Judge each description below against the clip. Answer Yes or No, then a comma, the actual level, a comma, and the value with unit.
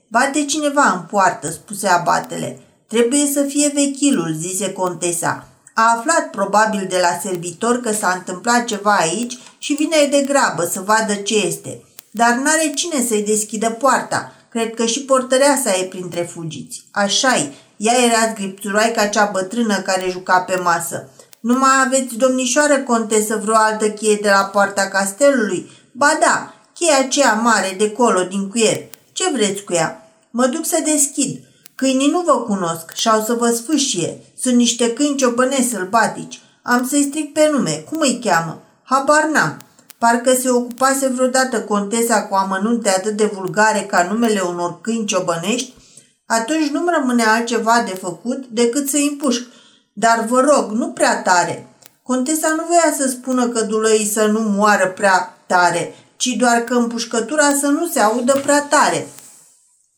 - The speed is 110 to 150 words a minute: No, average, 160 wpm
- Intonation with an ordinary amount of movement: Yes, average, 5.0 semitones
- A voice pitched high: Yes, high, 230 Hz